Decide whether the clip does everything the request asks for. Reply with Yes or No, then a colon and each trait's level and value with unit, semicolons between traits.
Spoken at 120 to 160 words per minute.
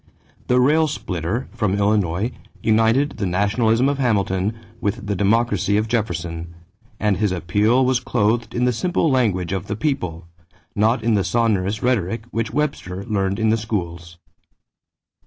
Yes: average, 150 wpm